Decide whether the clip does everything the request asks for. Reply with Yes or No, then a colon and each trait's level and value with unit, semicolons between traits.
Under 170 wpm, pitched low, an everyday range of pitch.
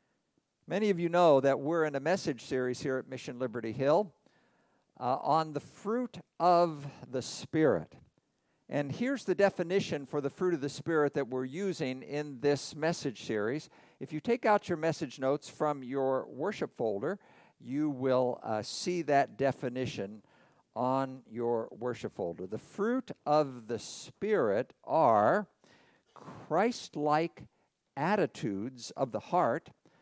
No: average, 145 wpm; medium, 145 Hz; average, 4.8 semitones